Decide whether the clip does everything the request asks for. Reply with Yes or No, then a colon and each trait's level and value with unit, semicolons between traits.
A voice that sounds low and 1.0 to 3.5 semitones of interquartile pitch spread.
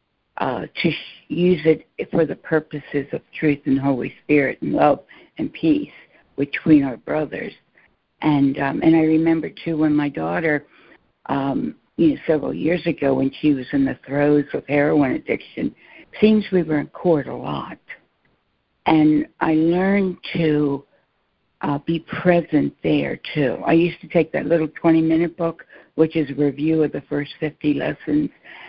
No: medium, 155 Hz; narrow, 2.4 semitones